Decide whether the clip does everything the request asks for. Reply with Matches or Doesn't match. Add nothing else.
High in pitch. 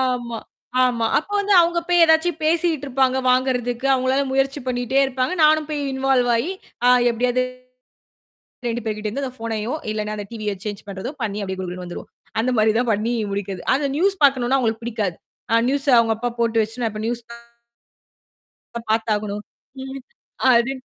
Matches